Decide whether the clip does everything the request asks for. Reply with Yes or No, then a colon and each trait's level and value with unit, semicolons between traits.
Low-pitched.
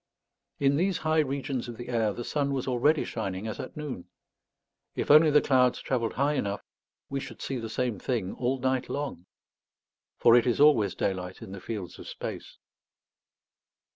Yes: low, 125 Hz